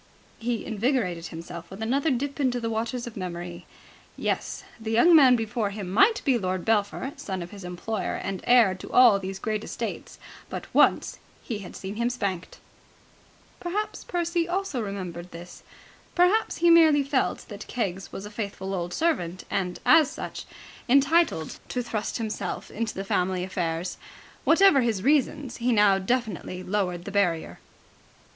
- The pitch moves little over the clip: No, wide, 5.6 semitones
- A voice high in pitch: Yes, high, 215 Hz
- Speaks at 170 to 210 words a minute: No, average, 160 wpm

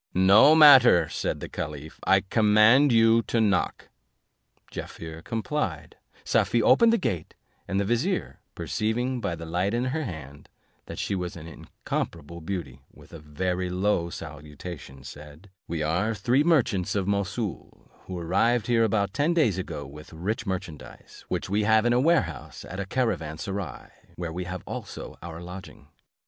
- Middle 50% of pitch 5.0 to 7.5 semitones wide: Yes, wide, 5.5 semitones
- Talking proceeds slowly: No, average, 160 wpm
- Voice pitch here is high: No, very low, 95 Hz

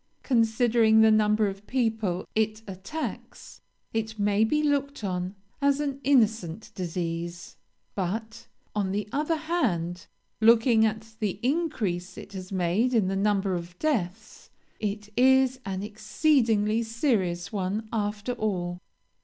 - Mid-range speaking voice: No, high, 215 Hz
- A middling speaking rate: No, slow, 130 wpm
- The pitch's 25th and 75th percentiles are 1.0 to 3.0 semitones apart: No, average, 3.7 semitones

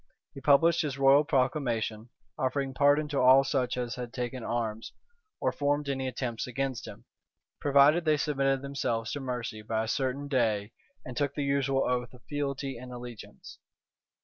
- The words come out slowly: No, average, 165 wpm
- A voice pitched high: No, low, 135 Hz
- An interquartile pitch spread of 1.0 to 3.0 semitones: Yes, narrow, 2.5 semitones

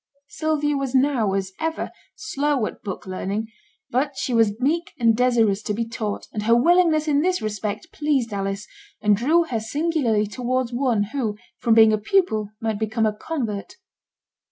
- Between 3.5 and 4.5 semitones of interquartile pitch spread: No, wide, 5.4 semitones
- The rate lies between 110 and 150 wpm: No, average, 170 wpm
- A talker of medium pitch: No, high, 235 Hz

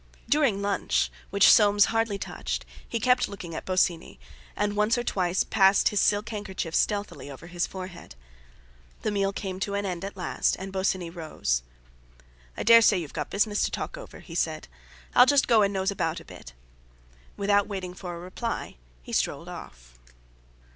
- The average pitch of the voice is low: No, high, 195 Hz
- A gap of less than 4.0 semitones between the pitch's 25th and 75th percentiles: Yes, average, 2.8 semitones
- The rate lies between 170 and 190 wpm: Yes, average, 175 wpm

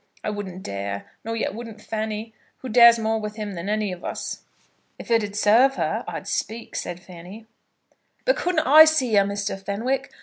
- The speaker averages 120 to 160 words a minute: No, average, 180 wpm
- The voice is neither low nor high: No, high, 215 Hz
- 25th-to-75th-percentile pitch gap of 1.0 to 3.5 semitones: Yes, average, 2.8 semitones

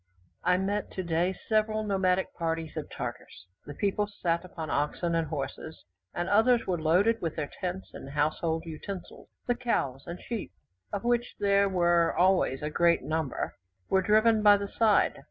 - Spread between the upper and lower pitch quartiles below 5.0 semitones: Yes, average, 4.1 semitones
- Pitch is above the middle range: No, medium, 180 Hz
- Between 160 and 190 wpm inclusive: Yes, average, 165 wpm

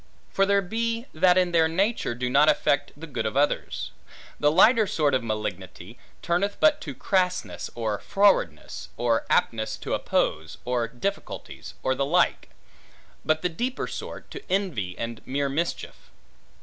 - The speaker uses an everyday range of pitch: No, wide, 8.5 semitones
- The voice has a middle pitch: Yes, medium, 155 Hz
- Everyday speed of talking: Yes, average, 160 wpm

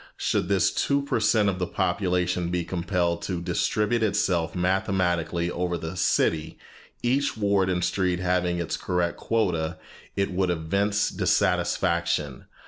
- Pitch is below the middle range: Yes, very low, 90 Hz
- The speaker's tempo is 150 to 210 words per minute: No, slow, 135 wpm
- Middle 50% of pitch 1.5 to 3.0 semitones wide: Yes, narrow, 2.4 semitones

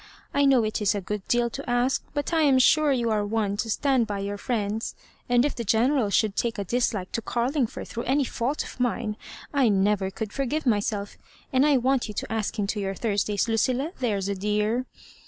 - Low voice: No, high, 230 Hz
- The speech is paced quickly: Yes, fast, 220 wpm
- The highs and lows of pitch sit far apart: No, average, 3.9 semitones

